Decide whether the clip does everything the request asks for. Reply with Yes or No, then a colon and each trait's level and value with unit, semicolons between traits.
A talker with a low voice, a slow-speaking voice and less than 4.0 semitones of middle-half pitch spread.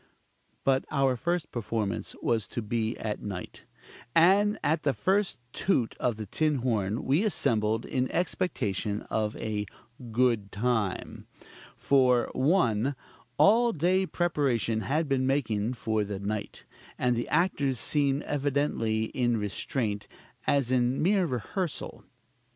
No: low, 125 Hz; slow, 130 wpm; average, 5.3 semitones